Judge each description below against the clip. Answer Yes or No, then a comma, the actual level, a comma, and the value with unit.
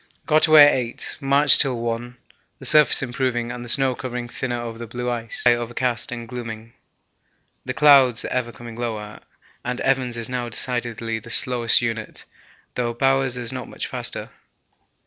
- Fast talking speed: No, average, 170 wpm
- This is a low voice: Yes, low, 120 Hz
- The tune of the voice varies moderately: No, narrow, 1.7 semitones